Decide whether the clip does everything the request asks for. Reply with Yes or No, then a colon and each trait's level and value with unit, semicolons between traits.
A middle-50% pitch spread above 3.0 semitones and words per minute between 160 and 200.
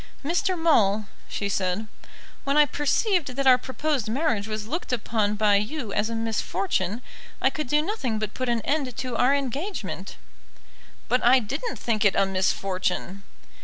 Yes: wide, 5.5 semitones; average, 165 wpm